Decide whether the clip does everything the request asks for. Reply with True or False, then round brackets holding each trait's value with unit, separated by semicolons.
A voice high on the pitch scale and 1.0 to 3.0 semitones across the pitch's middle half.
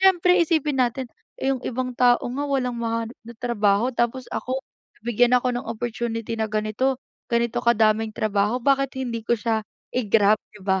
True (240 Hz; 2.7 semitones)